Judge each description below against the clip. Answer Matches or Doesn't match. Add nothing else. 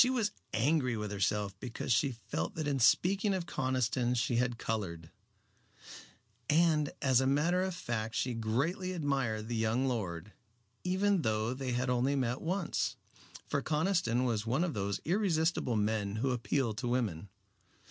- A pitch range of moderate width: Doesn't match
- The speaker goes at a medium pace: Matches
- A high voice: Doesn't match